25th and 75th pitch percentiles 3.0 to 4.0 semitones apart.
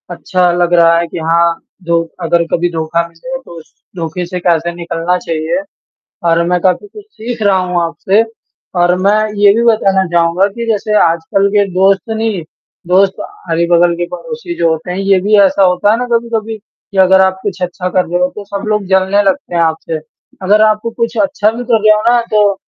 Yes: average, 3.7 semitones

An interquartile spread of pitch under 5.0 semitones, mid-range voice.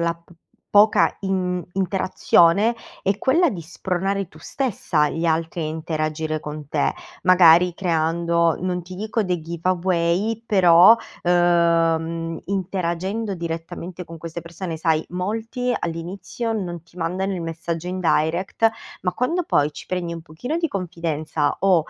Yes: narrow, 2.6 semitones; medium, 175 Hz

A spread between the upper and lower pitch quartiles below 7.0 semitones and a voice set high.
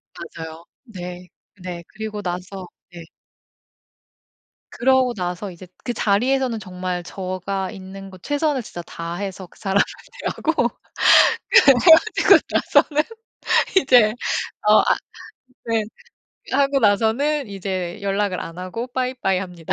Yes: average, 5.1 semitones; high, 195 Hz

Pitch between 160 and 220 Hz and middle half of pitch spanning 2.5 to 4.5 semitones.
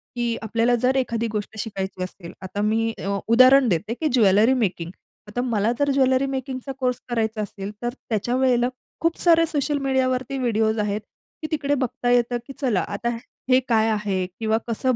No: high, 235 Hz; average, 3.5 semitones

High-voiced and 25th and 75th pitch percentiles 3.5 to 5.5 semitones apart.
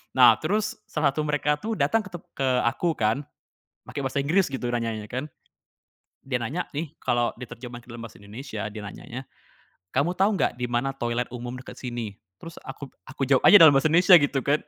No: low, 135 Hz; average, 4.1 semitones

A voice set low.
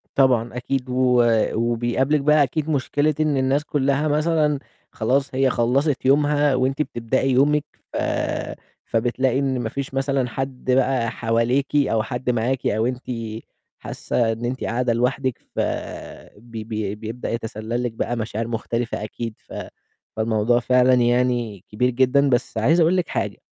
Yes: low, 125 Hz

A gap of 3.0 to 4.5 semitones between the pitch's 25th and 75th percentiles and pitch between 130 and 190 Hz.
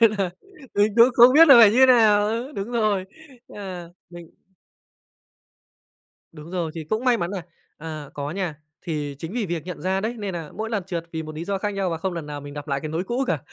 No: average, 5.1 semitones; medium, 185 Hz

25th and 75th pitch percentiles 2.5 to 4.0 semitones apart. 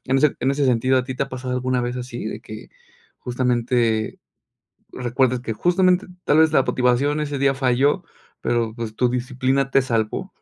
No: narrow, 2.1 semitones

